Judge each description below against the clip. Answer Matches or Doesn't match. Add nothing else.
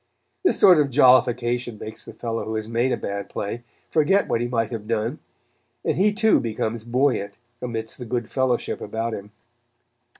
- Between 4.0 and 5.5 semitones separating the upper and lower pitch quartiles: Doesn't match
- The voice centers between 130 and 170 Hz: Doesn't match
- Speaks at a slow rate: Doesn't match